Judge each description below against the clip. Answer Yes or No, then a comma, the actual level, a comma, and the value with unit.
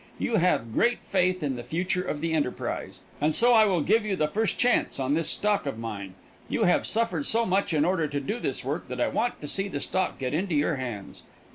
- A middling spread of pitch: No, wide, 5.7 semitones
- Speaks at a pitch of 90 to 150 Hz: No, medium, 165 Hz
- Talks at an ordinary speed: No, fast, 240 wpm